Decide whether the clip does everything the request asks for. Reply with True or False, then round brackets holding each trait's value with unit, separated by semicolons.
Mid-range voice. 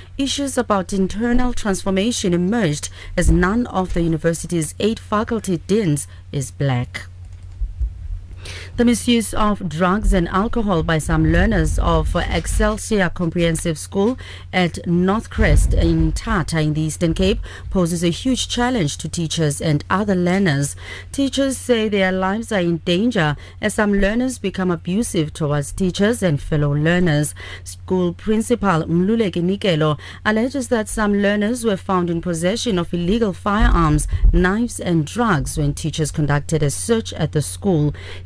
True (180 Hz)